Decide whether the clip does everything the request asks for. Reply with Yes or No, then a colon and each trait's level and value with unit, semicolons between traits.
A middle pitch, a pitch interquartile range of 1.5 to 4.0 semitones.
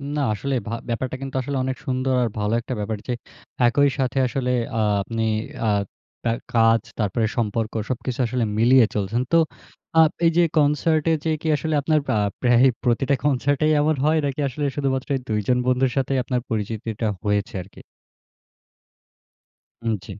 No: low, 125 Hz; average, 3.4 semitones